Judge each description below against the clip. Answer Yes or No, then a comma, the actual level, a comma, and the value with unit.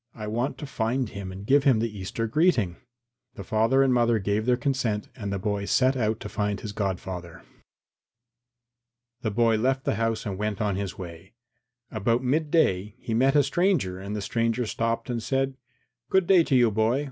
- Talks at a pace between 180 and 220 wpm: Yes, average, 195 wpm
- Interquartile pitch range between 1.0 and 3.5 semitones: No, average, 4.2 semitones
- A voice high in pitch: No, low, 115 Hz